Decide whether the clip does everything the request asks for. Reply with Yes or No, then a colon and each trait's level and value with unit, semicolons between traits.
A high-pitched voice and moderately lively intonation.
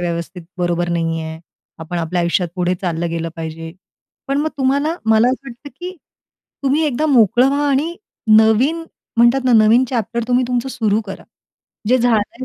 No: high, 230 Hz; wide, 7.2 semitones